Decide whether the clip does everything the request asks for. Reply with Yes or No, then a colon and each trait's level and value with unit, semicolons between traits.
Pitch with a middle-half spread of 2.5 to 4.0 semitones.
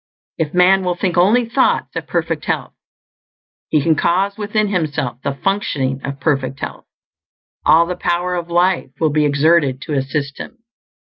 No: average, 4.5 semitones